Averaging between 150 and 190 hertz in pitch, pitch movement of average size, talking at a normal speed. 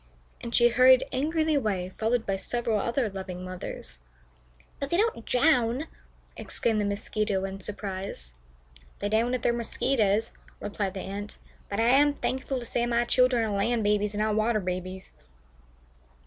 No: high, 220 Hz; average, 3.6 semitones; average, 160 wpm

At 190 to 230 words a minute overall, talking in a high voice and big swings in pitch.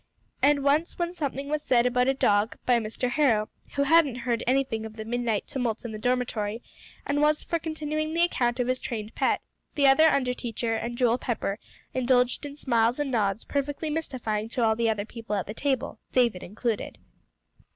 No: average, 195 wpm; very high, 250 Hz; average, 4.0 semitones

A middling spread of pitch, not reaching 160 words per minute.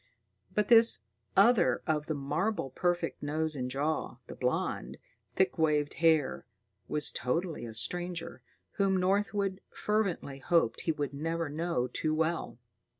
Yes: average, 4.1 semitones; slow, 135 wpm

